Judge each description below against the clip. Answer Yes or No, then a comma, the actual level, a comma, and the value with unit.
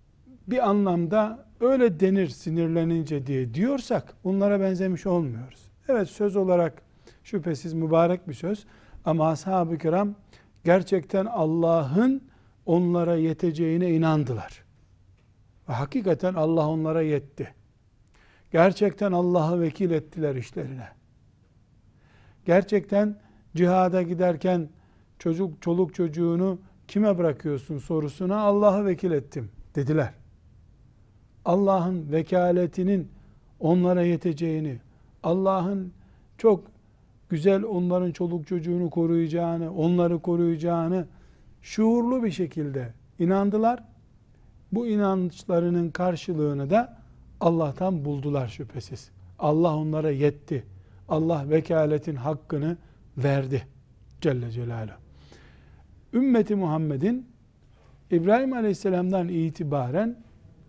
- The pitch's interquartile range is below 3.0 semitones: No, average, 4.6 semitones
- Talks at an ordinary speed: No, slow, 85 wpm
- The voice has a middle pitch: Yes, medium, 165 Hz